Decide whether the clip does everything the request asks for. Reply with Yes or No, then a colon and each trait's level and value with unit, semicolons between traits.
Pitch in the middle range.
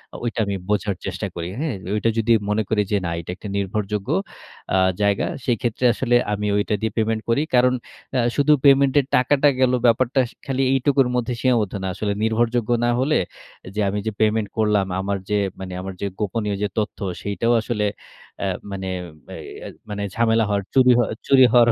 No: low, 110 Hz